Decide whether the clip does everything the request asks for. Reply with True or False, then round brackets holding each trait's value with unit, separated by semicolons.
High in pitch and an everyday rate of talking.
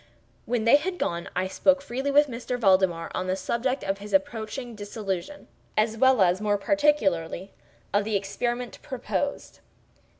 True (220 Hz; 155 wpm)